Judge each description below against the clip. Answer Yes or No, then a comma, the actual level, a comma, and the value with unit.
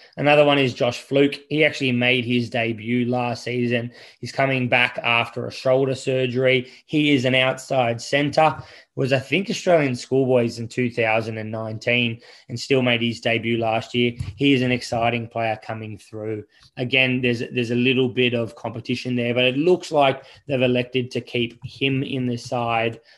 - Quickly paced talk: No, average, 180 wpm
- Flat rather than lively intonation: Yes, narrow, 2.2 semitones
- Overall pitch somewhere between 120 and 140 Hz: Yes, low, 125 Hz